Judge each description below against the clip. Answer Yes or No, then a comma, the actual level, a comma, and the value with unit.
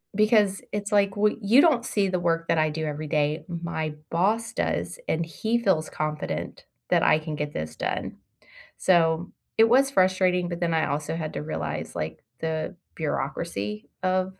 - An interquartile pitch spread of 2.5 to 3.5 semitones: No, average, 4.2 semitones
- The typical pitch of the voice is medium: Yes, medium, 170 Hz